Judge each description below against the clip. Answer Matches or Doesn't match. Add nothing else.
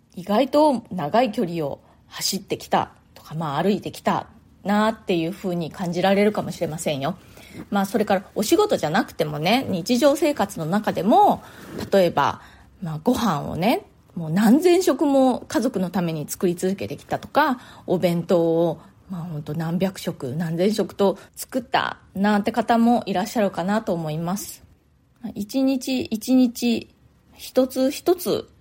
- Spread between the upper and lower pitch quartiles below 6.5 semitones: Matches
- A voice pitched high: Matches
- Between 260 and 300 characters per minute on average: Matches